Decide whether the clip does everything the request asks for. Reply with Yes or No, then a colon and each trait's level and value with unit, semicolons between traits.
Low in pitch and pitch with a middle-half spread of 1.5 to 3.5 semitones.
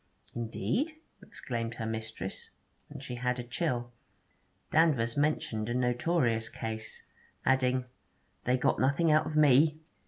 No: low, 125 Hz; average, 4.4 semitones